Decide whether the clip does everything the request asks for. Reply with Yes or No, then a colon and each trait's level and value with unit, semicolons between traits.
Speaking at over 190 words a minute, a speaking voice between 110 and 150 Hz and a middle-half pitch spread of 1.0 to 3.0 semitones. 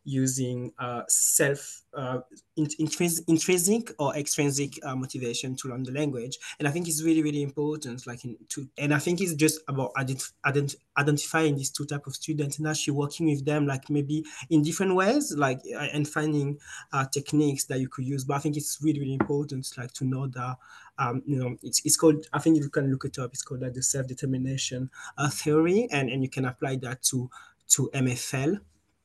Yes: average, 200 wpm; medium, 140 Hz; narrow, 2.6 semitones